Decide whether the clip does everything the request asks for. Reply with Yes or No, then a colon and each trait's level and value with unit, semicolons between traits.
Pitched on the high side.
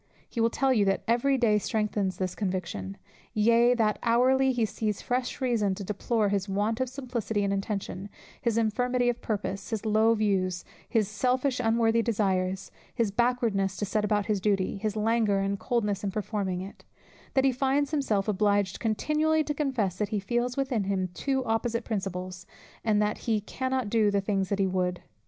Yes: high, 215 Hz